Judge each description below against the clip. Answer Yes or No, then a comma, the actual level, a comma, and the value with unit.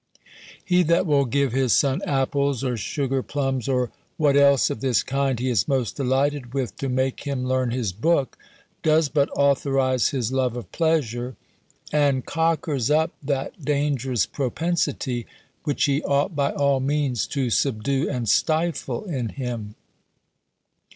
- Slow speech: No, average, 150 wpm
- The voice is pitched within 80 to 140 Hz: Yes, low, 135 Hz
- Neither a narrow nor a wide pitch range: No, narrow, 2.3 semitones